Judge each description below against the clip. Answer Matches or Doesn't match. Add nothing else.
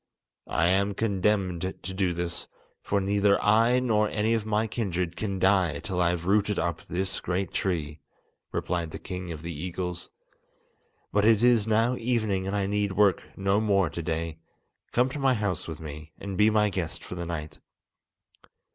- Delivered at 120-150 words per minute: Doesn't match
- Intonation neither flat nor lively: Matches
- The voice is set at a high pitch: Doesn't match